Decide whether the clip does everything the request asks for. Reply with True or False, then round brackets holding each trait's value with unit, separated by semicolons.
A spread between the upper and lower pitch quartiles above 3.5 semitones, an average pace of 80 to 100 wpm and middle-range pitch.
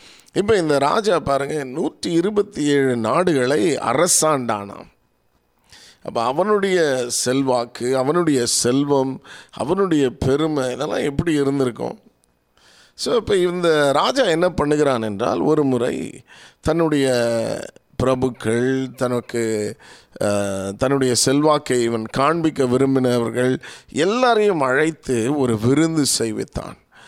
False (4.2 semitones; 90 wpm; 130 Hz)